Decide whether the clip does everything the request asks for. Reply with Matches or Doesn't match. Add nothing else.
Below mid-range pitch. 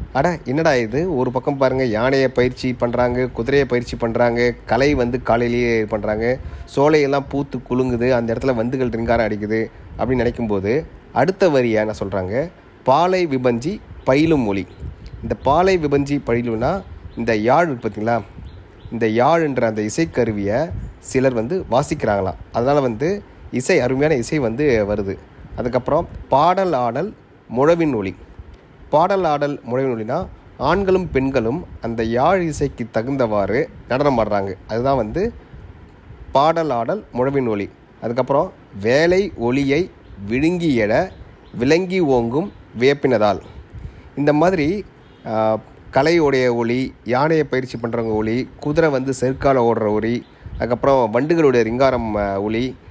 Matches